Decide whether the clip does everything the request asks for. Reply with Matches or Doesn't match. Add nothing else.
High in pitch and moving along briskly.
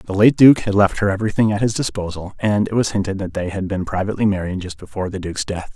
Doesn't match